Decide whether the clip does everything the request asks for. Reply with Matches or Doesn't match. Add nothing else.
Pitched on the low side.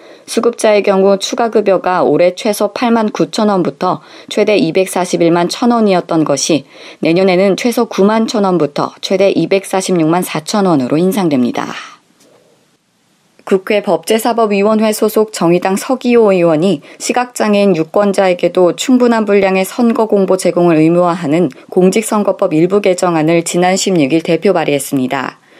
Doesn't match